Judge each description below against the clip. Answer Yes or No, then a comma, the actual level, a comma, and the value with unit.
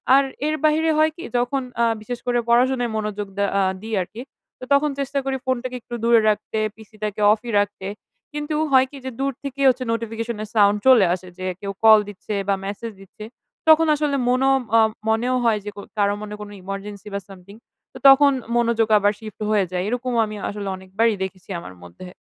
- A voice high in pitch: Yes, high, 225 Hz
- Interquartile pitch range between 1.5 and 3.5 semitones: No, average, 4.1 semitones